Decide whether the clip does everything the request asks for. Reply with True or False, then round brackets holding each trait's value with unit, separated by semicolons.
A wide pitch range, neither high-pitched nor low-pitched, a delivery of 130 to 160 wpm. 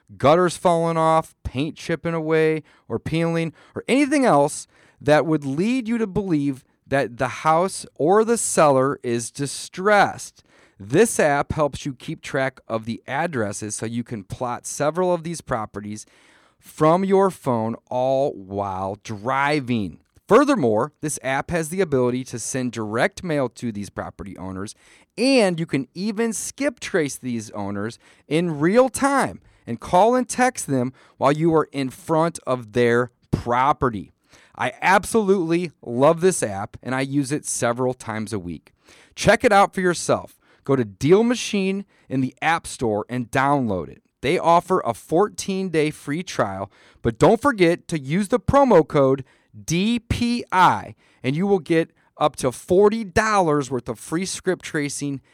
True (6.7 semitones; 145 Hz; 155 wpm)